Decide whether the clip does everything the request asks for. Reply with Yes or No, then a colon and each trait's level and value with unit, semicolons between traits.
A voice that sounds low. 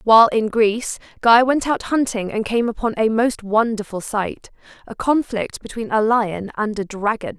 No: high, 225 Hz